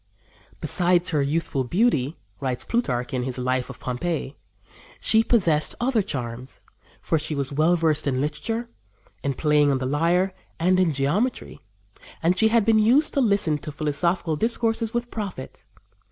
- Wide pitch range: Yes, wide, 7.3 semitones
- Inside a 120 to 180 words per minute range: Yes, average, 155 wpm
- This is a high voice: No, medium, 160 Hz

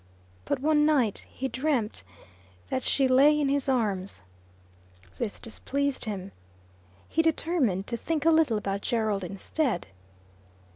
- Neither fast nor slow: No, slow, 130 wpm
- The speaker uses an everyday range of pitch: No, wide, 6.1 semitones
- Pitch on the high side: Yes, very high, 260 Hz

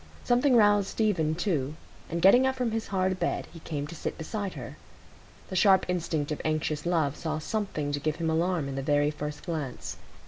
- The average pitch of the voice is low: No, medium, 165 Hz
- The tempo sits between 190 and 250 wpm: Yes, average, 200 wpm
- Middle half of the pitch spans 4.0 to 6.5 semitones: Yes, average, 4.7 semitones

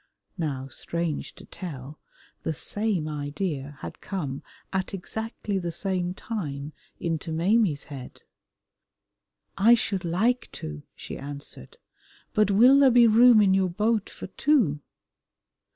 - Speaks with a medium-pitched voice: Yes, medium, 180 Hz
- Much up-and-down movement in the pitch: Yes, wide, 6.4 semitones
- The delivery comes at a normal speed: No, slow, 125 wpm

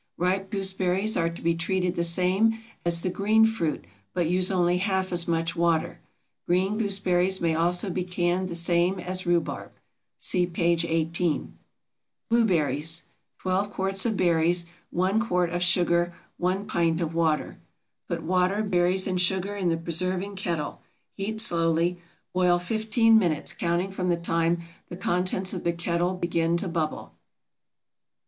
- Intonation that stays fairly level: Yes, narrow, 1.9 semitones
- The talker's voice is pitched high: No, medium, 180 Hz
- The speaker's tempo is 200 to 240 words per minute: No, average, 150 wpm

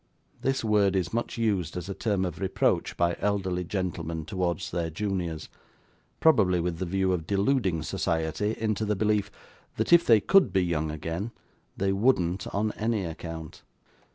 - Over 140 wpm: Yes, average, 160 wpm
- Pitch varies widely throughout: No, average, 3.7 semitones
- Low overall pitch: Yes, very low, 95 Hz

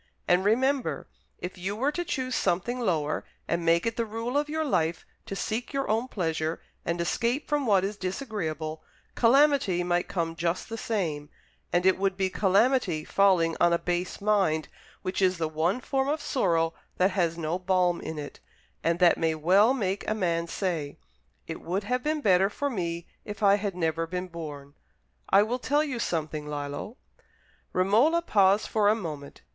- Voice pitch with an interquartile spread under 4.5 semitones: No, average, 5.3 semitones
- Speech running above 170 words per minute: Yes, average, 180 wpm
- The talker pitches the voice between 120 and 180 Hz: No, high, 190 Hz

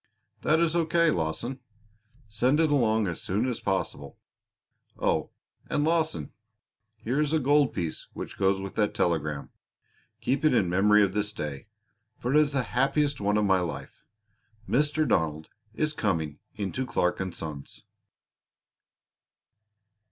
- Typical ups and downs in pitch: No, wide, 8.6 semitones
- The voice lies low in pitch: Yes, low, 105 Hz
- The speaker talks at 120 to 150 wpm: Yes, average, 145 wpm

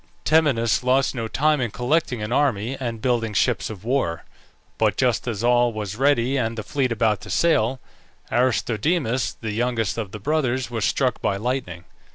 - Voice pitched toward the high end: No, low, 120 Hz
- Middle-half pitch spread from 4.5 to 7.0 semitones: No, average, 3.2 semitones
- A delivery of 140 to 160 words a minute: No, average, 175 wpm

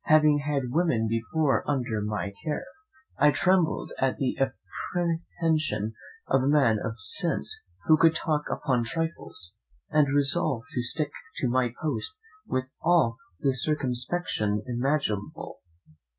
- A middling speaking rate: No, slow, 125 wpm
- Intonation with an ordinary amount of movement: Yes, average, 4.6 semitones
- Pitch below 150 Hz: Yes, low, 135 Hz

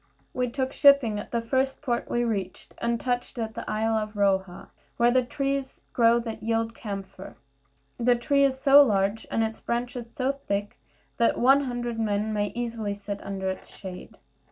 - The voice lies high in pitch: Yes, high, 230 Hz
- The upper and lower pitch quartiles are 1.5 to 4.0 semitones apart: Yes, average, 3.2 semitones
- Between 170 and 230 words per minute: Yes, average, 180 wpm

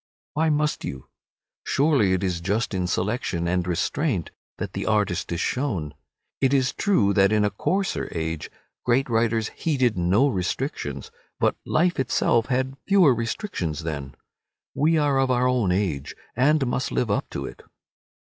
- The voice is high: No, low, 115 Hz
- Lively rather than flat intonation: Yes, wide, 7.0 semitones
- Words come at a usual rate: Yes, average, 155 wpm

